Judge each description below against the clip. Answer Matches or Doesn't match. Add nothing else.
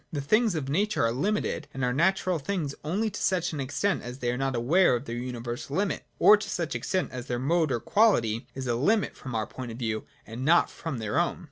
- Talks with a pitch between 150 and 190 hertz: Doesn't match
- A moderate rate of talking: Doesn't match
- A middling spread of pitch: Doesn't match